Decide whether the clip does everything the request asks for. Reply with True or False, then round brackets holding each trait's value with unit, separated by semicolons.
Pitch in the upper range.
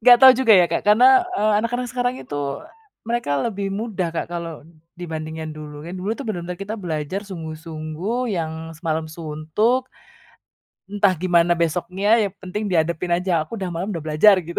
False (180 Hz)